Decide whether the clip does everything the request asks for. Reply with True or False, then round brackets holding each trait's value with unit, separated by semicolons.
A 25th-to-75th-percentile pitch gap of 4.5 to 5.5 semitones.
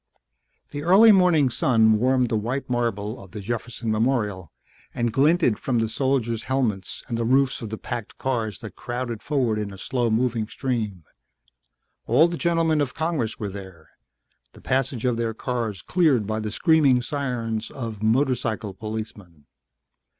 False (3.6 semitones)